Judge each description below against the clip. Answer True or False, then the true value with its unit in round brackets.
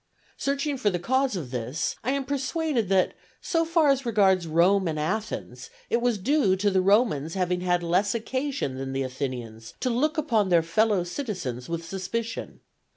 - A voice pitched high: True (195 Hz)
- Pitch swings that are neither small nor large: False (7.4 semitones)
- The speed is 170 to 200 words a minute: True (175 wpm)